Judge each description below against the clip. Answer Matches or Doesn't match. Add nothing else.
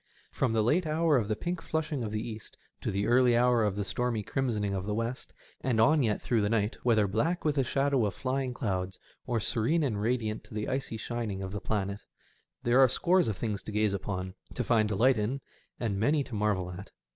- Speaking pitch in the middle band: Doesn't match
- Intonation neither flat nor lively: Matches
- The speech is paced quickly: Matches